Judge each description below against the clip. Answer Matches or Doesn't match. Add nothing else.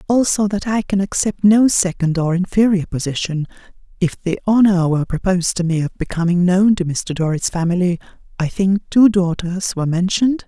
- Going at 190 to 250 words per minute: Doesn't match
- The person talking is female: Matches